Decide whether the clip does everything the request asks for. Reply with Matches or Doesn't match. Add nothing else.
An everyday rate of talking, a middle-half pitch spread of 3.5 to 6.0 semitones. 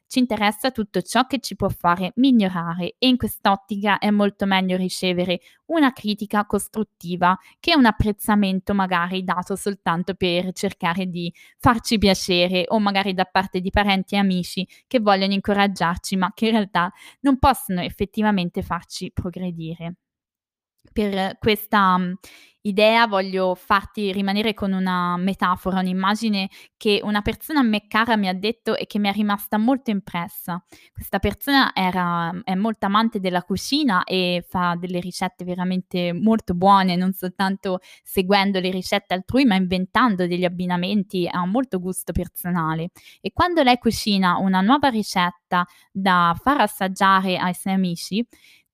Doesn't match